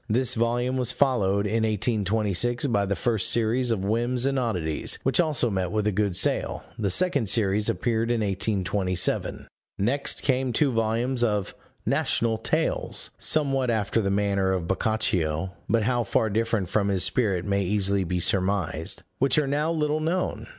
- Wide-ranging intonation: No, average, 3.8 semitones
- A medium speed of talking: Yes, average, 165 wpm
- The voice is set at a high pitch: No, low, 110 Hz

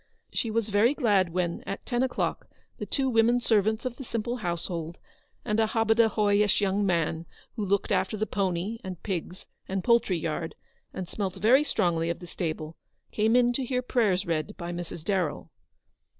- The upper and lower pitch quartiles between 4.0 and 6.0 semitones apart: Yes, average, 4.7 semitones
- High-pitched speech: Yes, high, 205 Hz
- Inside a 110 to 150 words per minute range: No, average, 175 wpm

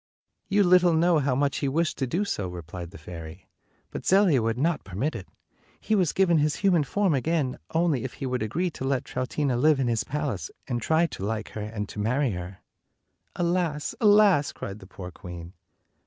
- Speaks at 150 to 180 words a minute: No, average, 200 wpm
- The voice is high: No, medium, 140 Hz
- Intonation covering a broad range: Yes, wide, 7.9 semitones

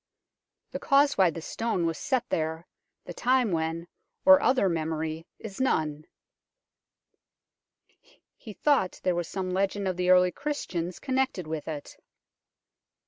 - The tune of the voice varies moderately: No, wide, 6.9 semitones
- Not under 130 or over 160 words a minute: Yes, slow, 135 wpm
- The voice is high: No, medium, 180 Hz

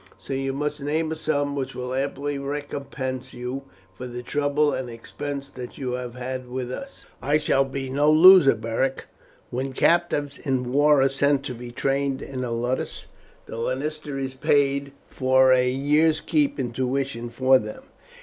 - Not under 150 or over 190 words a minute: Yes, average, 170 wpm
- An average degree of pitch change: No, narrow, 2.1 semitones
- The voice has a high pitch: No, low, 135 Hz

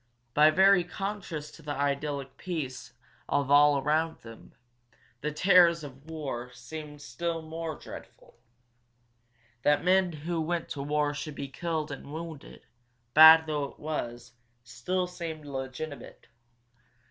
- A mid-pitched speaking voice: Yes, medium, 150 Hz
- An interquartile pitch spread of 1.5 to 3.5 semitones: Yes, average, 2.8 semitones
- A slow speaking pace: Yes, slow, 125 wpm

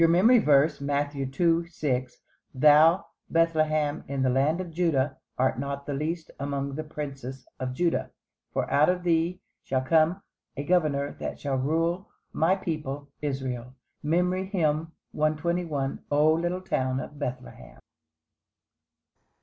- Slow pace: Yes, slow, 130 wpm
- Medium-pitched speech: Yes, medium, 150 Hz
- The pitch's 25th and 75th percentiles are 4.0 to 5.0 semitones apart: No, average, 3.4 semitones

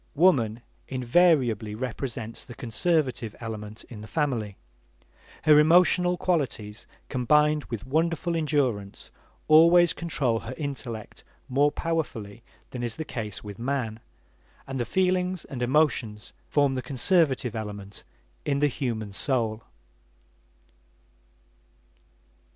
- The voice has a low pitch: Yes, low, 130 Hz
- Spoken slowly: Yes, slow, 110 wpm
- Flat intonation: No, wide, 5.6 semitones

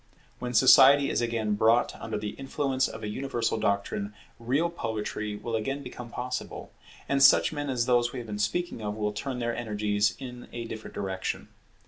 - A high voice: No, low, 120 Hz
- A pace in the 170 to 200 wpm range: Yes, average, 180 wpm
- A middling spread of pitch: Yes, average, 3.6 semitones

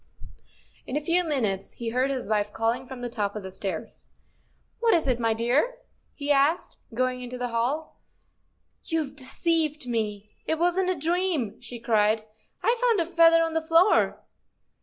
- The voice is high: Yes, very high, 265 Hz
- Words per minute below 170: No, average, 185 wpm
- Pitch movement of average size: No, wide, 6.2 semitones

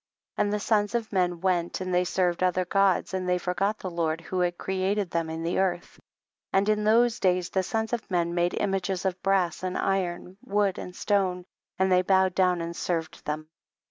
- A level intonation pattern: Yes, narrow, 1.8 semitones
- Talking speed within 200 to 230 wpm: Yes, fast, 205 wpm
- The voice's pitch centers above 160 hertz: Yes, medium, 185 Hz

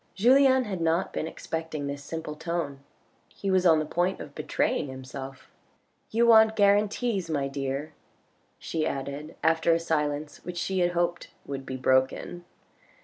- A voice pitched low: No, medium, 165 Hz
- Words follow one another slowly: No, average, 155 wpm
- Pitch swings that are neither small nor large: Yes, average, 4.9 semitones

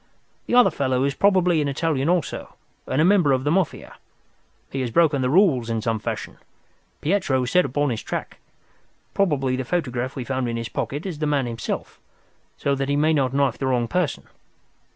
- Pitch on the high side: No, medium, 140 Hz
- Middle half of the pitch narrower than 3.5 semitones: No, average, 4.1 semitones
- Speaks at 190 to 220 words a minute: Yes, average, 195 wpm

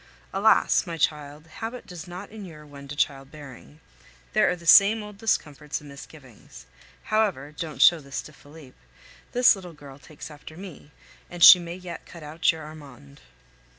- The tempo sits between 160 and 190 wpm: Yes, average, 170 wpm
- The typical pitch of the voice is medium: Yes, medium, 155 Hz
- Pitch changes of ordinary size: Yes, average, 3.8 semitones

